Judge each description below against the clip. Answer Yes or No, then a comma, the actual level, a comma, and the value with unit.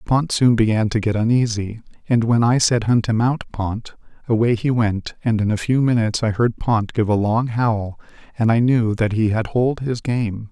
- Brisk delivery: Yes, fast, 215 wpm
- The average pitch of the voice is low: Yes, low, 115 Hz